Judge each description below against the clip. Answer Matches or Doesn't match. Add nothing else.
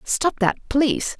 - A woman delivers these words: Matches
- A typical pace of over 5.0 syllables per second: Doesn't match